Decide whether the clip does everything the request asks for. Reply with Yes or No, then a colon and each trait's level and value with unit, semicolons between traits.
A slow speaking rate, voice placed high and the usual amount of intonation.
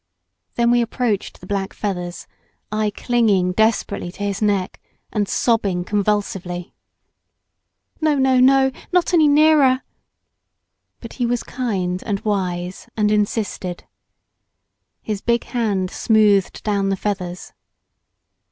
Yes: slow, 115 wpm; high, 210 Hz; average, 3.8 semitones